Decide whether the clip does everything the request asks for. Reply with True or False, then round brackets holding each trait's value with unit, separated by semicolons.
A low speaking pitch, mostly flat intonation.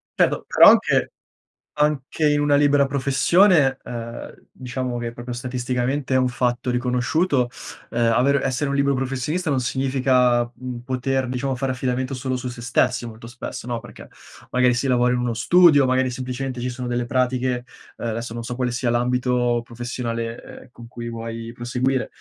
True (125 Hz; 1.7 semitones)